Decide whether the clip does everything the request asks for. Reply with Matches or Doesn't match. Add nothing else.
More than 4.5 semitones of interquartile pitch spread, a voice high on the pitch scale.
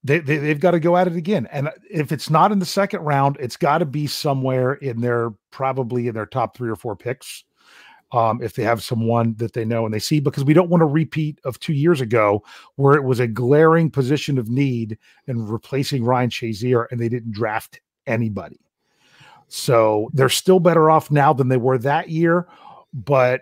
Doesn't match